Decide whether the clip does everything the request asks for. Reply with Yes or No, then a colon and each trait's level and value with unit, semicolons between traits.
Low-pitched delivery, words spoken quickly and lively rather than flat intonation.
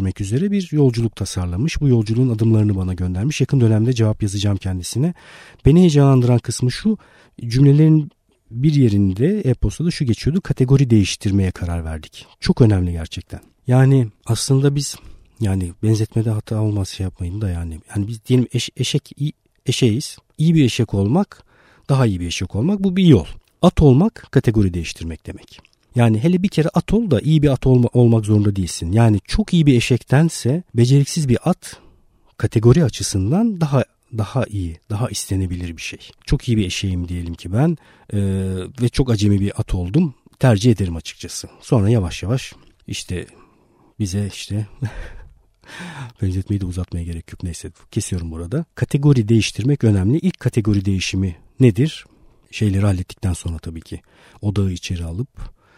Yes: low, 115 Hz; fast, 155 wpm; wide, 6.0 semitones